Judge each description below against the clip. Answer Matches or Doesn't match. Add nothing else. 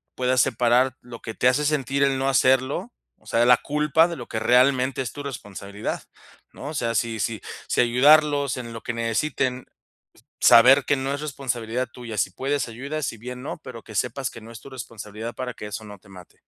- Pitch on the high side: Doesn't match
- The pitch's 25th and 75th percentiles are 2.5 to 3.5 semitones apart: Matches